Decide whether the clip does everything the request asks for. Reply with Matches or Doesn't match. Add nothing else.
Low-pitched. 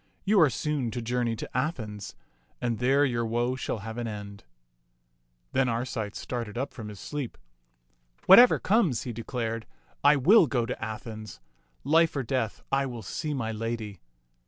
Matches